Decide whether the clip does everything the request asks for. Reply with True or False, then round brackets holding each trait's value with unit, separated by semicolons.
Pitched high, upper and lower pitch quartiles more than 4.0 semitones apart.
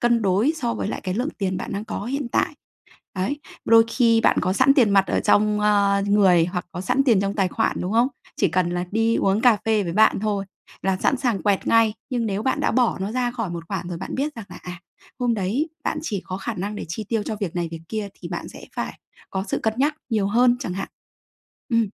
False (210 Hz; 3.5 semitones)